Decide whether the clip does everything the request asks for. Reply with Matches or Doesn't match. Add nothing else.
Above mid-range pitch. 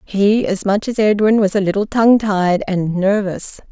Matches